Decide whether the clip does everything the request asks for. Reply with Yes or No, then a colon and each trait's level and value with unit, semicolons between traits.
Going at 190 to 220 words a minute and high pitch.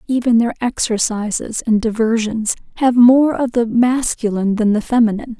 No: average, 145 wpm; high, 230 Hz